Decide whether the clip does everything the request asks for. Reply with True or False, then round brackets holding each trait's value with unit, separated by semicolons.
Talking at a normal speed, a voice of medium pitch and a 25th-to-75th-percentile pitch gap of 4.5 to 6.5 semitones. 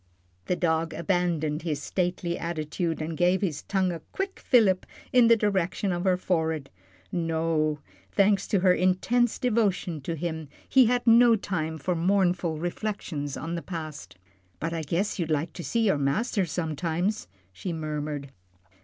False (155 wpm; 175 Hz; 3.5 semitones)